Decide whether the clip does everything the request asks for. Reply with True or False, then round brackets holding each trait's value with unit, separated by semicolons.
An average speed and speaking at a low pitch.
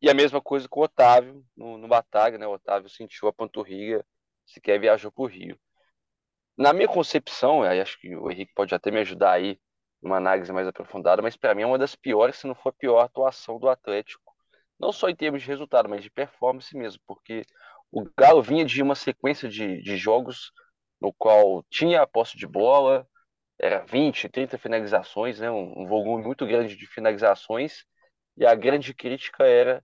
False (195 wpm; 120 Hz)